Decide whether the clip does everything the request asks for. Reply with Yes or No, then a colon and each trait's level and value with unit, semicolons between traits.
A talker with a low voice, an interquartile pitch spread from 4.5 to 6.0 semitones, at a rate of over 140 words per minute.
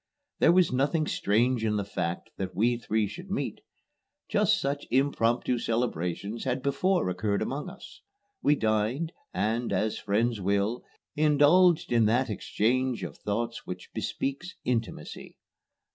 No: low, 120 Hz; average, 5.2 semitones; slow, 135 wpm